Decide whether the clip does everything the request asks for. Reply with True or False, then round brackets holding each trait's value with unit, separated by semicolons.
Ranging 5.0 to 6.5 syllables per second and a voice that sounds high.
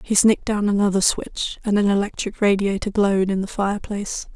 True (5.8 syllables/s; 200 Hz)